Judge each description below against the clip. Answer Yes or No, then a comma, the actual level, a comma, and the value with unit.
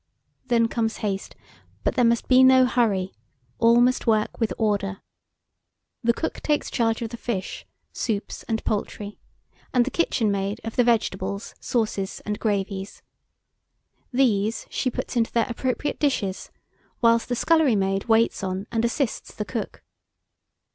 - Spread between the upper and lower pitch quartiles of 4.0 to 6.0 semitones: No, average, 3.2 semitones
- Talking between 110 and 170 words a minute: Yes, average, 150 wpm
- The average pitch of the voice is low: No, high, 225 Hz